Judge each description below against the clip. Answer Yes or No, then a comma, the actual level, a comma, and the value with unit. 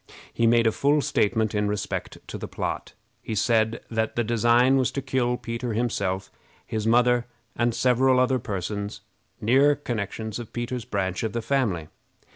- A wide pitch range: No, narrow, 2.6 semitones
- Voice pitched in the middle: No, low, 115 Hz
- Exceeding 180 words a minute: No, average, 165 wpm